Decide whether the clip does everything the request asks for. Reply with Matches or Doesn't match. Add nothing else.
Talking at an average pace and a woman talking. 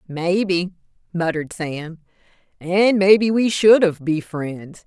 Doesn't match